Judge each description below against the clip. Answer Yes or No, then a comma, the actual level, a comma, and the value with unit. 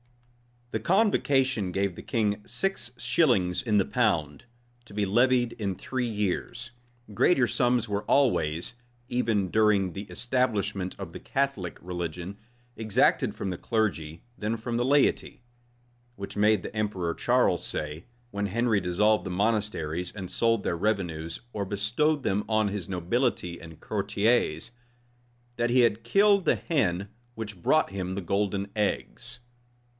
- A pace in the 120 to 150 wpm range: Yes, average, 140 wpm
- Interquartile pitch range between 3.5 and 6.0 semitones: Yes, average, 4.3 semitones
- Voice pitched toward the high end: No, low, 105 Hz